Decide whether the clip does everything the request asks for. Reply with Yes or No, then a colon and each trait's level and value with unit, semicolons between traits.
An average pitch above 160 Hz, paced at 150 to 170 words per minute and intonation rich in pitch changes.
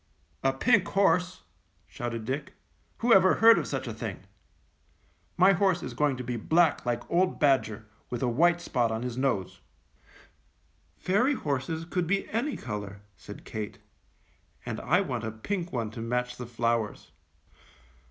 No: low, 135 Hz; average, 155 wpm; wide, 7.5 semitones